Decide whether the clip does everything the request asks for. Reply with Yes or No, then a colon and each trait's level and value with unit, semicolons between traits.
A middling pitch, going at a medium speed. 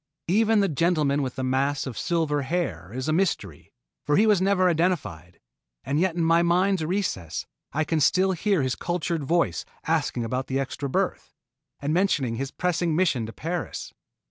Yes: medium, 160 Hz; average, 175 wpm